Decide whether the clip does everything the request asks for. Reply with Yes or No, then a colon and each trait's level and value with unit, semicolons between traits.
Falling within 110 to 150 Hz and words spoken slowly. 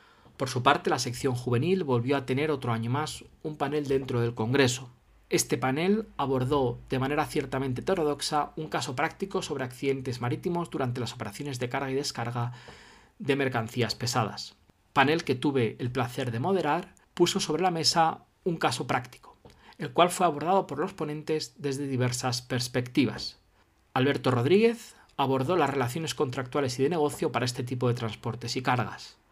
No: low, 135 Hz; average, 165 wpm